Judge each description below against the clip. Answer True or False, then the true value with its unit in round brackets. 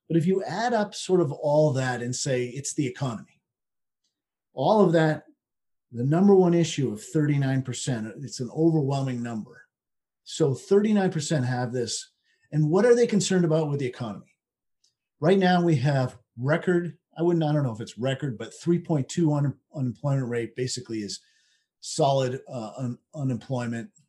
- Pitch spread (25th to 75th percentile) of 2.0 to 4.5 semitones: False (4.9 semitones)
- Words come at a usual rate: True (175 wpm)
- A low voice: False (145 Hz)